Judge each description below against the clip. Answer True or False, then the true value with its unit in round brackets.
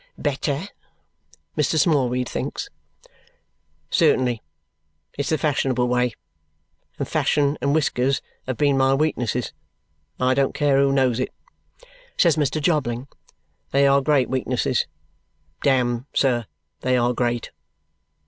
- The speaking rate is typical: False (120 wpm)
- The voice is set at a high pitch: False (135 Hz)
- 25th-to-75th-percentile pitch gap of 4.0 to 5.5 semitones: False (2.4 semitones)